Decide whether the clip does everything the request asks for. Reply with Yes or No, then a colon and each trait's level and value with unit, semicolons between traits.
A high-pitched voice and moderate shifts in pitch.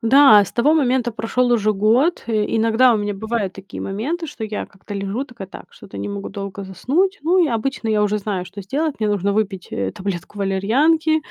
Yes: high, 220 Hz; average, 4.5 semitones